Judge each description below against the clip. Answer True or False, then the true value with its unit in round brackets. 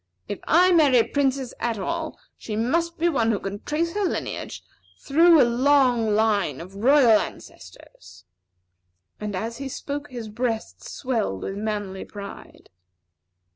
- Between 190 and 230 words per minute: False (150 wpm)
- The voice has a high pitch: True (235 Hz)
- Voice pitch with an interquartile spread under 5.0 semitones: False (5.5 semitones)